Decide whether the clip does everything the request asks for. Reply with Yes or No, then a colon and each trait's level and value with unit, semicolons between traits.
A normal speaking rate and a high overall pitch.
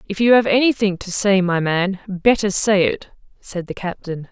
Yes: average, 195 wpm; high, 195 Hz